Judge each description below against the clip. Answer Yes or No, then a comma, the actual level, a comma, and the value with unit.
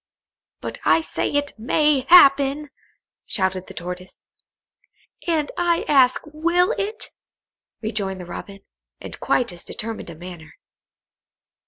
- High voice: Yes, very high, 260 Hz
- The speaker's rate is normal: No, slow, 120 wpm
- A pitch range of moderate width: No, wide, 8.3 semitones